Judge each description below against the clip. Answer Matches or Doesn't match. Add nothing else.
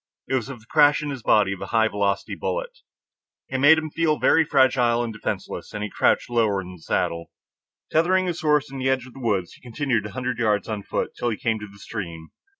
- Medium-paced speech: Doesn't match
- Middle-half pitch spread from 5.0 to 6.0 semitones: Matches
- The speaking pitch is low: Matches